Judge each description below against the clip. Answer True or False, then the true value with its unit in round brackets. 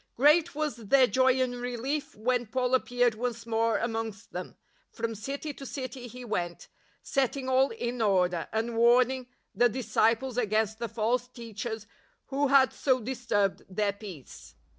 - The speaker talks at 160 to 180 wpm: False (150 wpm)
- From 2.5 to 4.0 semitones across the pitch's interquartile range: True (2.8 semitones)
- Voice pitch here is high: True (240 Hz)